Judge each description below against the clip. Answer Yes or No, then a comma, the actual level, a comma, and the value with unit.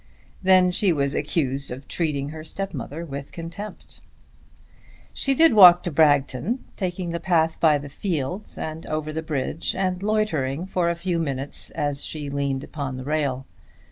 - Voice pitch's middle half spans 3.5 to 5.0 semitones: Yes, average, 4.4 semitones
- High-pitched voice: No, medium, 160 Hz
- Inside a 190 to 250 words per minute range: No, average, 160 wpm